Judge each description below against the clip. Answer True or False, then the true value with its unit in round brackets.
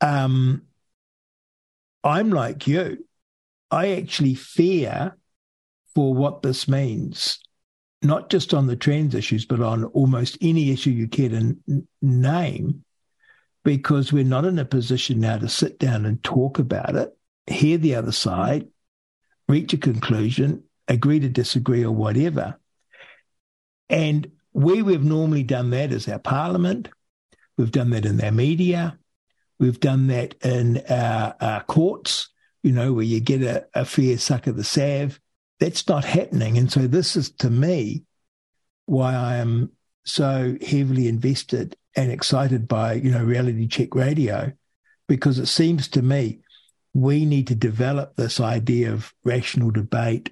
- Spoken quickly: False (145 wpm)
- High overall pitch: False (135 Hz)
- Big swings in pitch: False (3.7 semitones)